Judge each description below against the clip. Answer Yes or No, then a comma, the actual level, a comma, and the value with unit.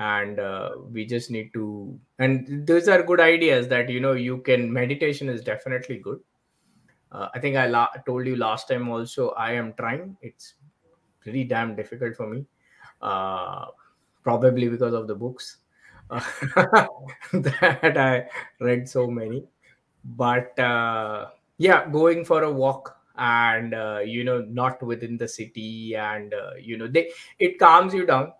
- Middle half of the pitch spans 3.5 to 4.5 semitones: No, average, 2.7 semitones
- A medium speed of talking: Yes, average, 160 wpm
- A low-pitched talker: Yes, low, 125 Hz